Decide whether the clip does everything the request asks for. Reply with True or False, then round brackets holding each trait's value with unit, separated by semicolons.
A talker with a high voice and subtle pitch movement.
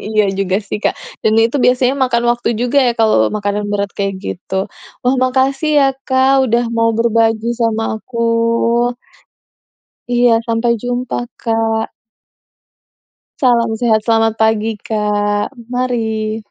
True (225 Hz; 2.2 semitones)